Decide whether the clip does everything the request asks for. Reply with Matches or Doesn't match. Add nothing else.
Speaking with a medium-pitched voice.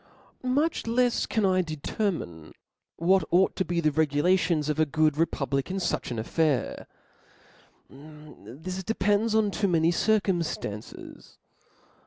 Matches